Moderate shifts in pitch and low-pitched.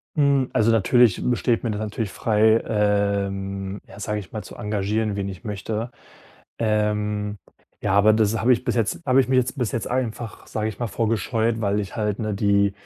No: narrow, 2.1 semitones; low, 105 Hz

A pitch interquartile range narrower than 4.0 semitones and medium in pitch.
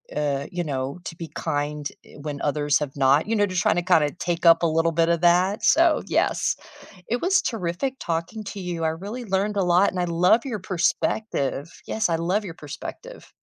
No: average, 4.6 semitones; medium, 175 Hz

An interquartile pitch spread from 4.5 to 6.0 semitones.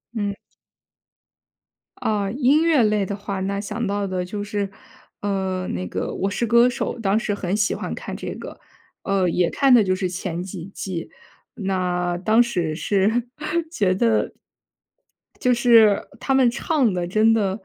No: average, 3.6 semitones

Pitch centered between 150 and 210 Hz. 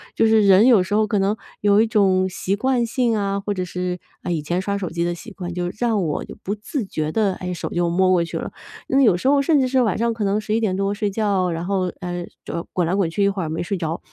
Yes: high, 195 Hz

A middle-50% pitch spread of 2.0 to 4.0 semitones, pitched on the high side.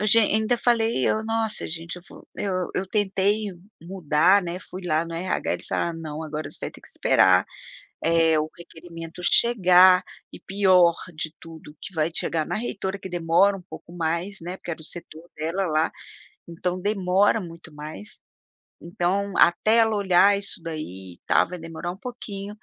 No: average, 3.4 semitones; medium, 180 Hz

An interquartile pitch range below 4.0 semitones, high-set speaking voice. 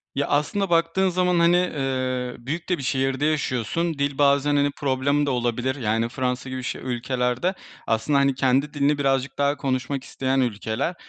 No: narrow, 2.4 semitones; low, 135 Hz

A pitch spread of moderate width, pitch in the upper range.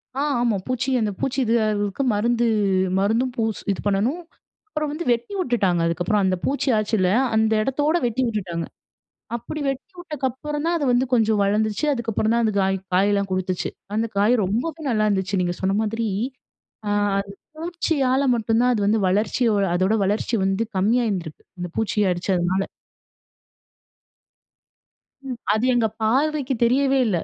Yes: average, 4.5 semitones; high, 220 Hz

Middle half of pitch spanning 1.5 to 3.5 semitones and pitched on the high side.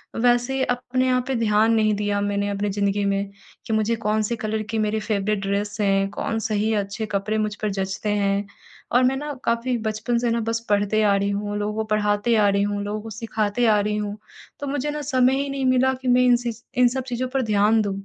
Yes: average, 2.9 semitones; high, 215 Hz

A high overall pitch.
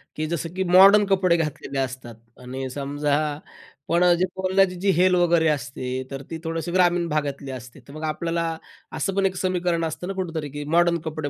No: medium, 165 Hz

